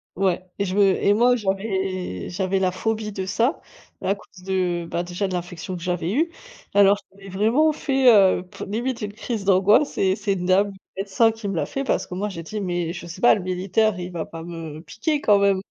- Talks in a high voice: Yes, high, 195 Hz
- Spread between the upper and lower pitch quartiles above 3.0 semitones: No, average, 2.7 semitones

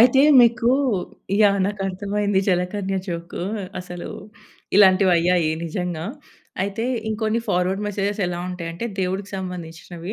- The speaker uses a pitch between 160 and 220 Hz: Yes, high, 190 Hz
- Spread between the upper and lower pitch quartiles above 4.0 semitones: No, narrow, 2.6 semitones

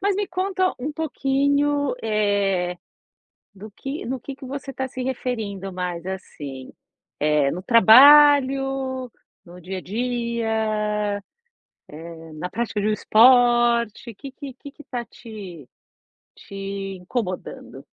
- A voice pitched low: No, high, 235 Hz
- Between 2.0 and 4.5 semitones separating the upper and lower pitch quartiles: No, wide, 5.6 semitones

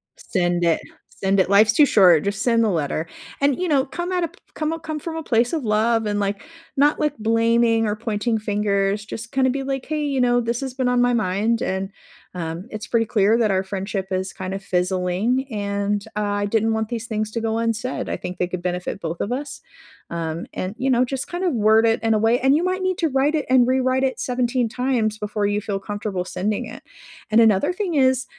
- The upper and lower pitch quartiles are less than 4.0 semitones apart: No, average, 4.4 semitones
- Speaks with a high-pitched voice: Yes, high, 225 Hz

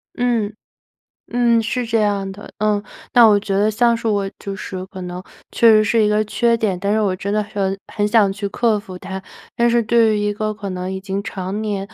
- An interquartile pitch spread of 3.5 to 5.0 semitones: No, narrow, 2.4 semitones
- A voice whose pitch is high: Yes, high, 210 Hz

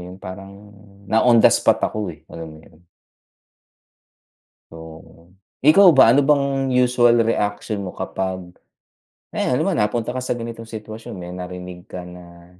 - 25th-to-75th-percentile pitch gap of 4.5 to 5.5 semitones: Yes, average, 5.0 semitones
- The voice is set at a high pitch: No, low, 105 Hz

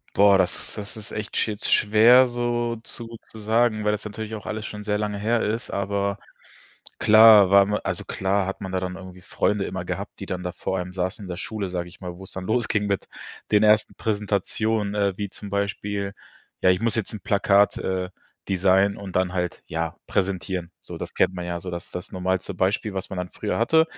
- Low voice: Yes, low, 100 Hz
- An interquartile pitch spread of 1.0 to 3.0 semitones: Yes, narrow, 2.4 semitones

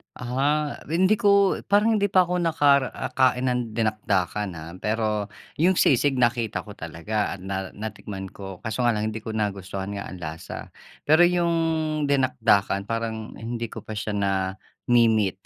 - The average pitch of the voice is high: No, low, 110 Hz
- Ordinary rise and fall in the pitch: No, wide, 5.9 semitones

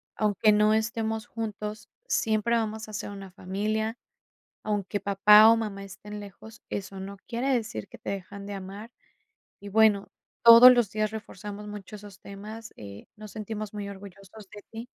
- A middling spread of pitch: No, narrow, 1.7 semitones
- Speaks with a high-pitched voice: Yes, high, 210 Hz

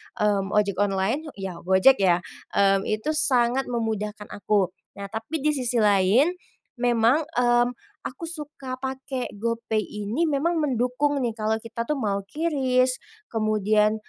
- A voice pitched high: Yes, high, 230 Hz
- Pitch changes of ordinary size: Yes, average, 4.3 semitones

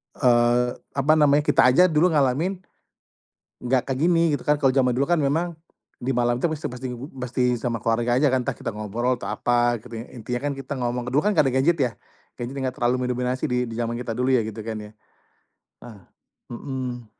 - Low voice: Yes, low, 125 Hz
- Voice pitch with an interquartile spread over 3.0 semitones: No, average, 2.7 semitones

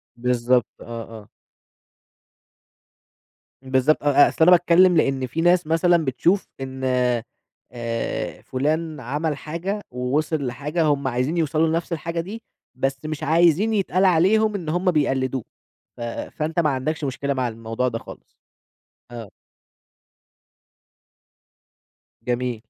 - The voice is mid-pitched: Yes, medium, 150 Hz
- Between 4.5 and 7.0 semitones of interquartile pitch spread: Yes, average, 4.8 semitones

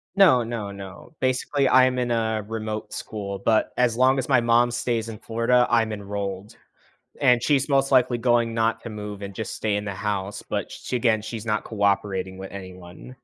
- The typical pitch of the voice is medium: No, low, 115 Hz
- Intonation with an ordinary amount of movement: Yes, average, 3.2 semitones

